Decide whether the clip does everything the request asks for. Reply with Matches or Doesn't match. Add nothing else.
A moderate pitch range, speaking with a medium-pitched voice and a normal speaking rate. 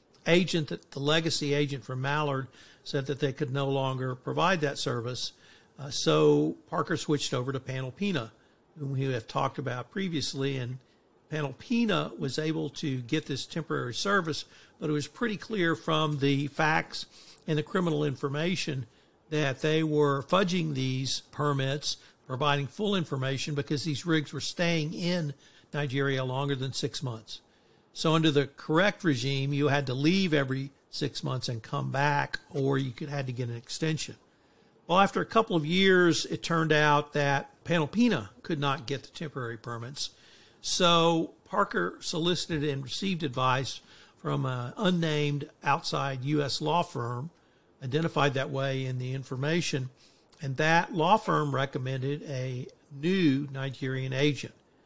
Matches